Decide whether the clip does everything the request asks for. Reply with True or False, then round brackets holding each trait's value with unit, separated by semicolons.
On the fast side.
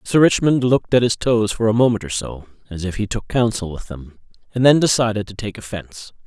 True (230 wpm)